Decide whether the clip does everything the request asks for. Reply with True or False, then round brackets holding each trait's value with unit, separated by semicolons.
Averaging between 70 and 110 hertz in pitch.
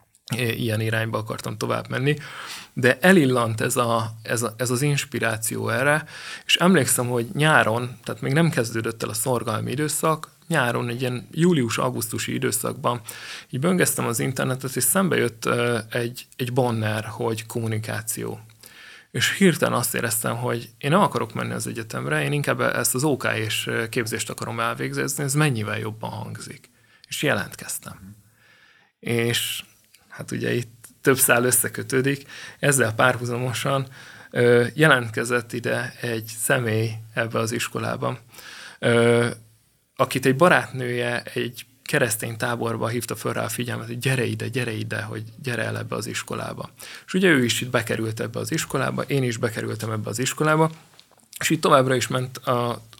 False (120 Hz)